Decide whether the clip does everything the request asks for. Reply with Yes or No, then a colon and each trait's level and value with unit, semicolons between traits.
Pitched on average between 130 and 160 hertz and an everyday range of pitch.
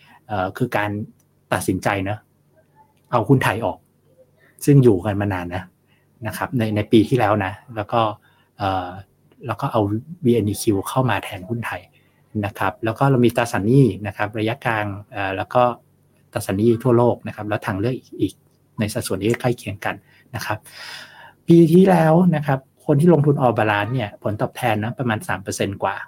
No: low, 110 Hz; average, 3.8 semitones